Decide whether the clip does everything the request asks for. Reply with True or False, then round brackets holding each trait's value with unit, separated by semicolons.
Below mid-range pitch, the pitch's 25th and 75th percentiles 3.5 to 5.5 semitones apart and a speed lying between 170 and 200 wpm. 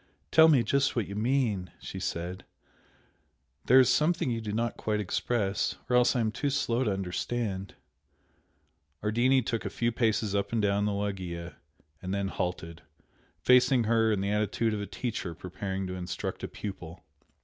True (105 Hz; 3.9 semitones; 175 wpm)